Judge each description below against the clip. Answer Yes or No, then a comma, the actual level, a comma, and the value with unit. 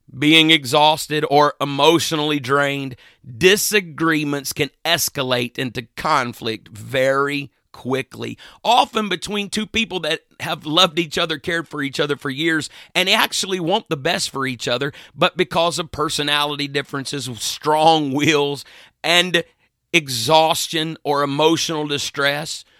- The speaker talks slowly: Yes, slow, 125 wpm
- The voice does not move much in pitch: No, average, 3.2 semitones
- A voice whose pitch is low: No, medium, 150 Hz